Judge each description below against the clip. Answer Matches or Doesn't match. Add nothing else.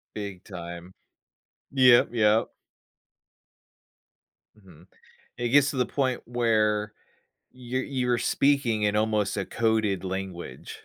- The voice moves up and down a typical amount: Matches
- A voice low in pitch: Matches